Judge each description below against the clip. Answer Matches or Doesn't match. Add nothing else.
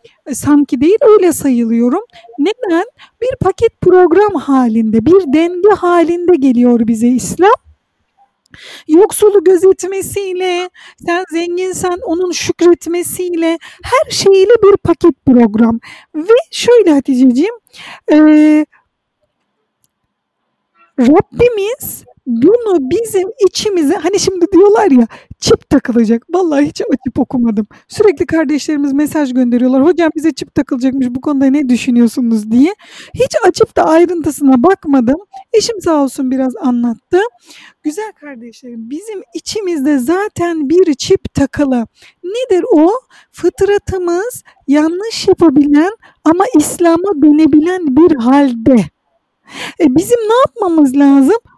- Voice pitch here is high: Matches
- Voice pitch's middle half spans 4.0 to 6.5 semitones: Matches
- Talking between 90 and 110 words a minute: Matches